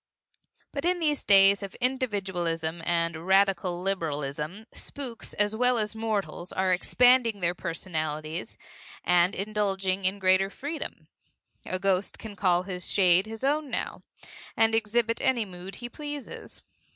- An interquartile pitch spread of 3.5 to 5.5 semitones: Yes, average, 4.2 semitones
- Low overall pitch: No, high, 195 Hz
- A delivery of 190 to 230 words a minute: No, slow, 135 wpm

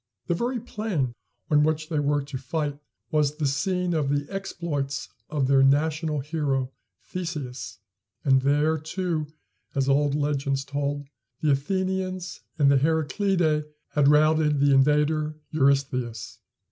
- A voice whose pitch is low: No, medium, 150 Hz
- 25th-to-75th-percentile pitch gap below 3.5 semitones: Yes, narrow, 2.4 semitones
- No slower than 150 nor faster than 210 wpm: No, slow, 135 wpm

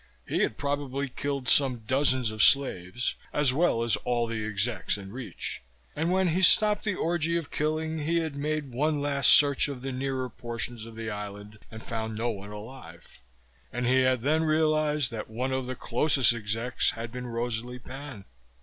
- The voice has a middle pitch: No, low, 130 Hz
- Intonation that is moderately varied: Yes, average, 4.3 semitones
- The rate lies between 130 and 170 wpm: No, average, 185 wpm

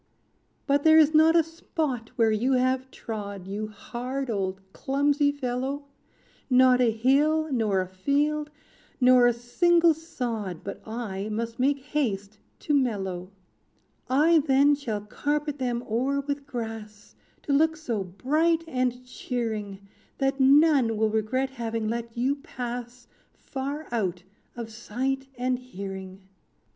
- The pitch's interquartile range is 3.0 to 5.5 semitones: Yes, average, 4.4 semitones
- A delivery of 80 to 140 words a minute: Yes, slow, 135 wpm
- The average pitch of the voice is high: Yes, very high, 250 Hz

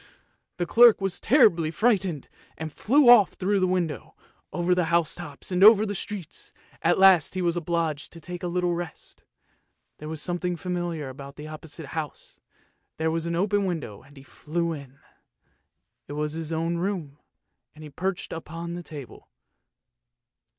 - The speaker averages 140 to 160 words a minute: No, average, 170 wpm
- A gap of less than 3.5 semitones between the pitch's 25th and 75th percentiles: Yes, average, 3.0 semitones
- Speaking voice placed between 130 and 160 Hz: No, medium, 170 Hz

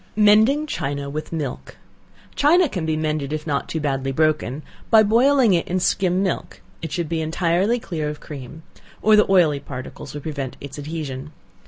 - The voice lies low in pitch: No, medium, 160 Hz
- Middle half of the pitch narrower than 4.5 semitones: No, average, 5.1 semitones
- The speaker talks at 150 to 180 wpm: Yes, average, 175 wpm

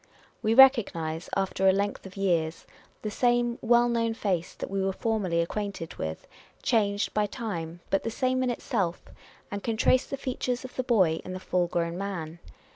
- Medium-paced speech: Yes, average, 185 wpm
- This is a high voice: Yes, high, 200 Hz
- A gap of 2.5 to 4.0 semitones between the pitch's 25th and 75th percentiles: No, average, 5.1 semitones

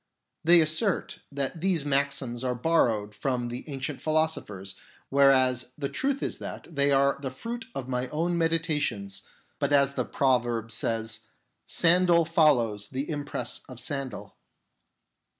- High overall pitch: No, medium, 140 Hz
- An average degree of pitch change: Yes, average, 4.3 semitones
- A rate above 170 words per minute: No, average, 140 wpm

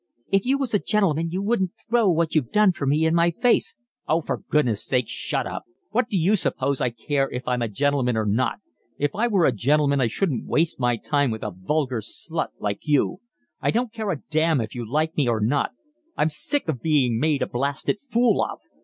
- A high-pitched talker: No, medium, 150 Hz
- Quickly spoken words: Yes, fast, 220 wpm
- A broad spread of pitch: Yes, wide, 6.8 semitones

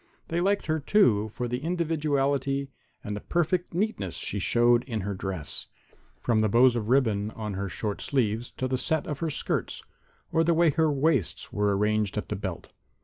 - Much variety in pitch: Yes, wide, 7.0 semitones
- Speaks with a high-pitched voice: No, low, 125 Hz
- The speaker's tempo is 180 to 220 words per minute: Yes, average, 185 wpm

